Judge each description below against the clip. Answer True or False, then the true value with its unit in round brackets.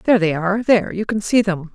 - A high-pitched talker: True (200 Hz)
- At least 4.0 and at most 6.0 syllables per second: False (6.4 syllables/s)